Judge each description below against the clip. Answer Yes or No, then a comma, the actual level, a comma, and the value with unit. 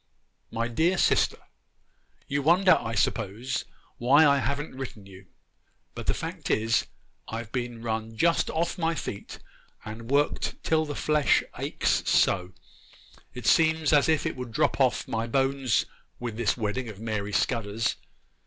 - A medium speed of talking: Yes, average, 150 wpm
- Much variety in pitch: No, average, 4.7 semitones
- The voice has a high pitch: No, low, 120 Hz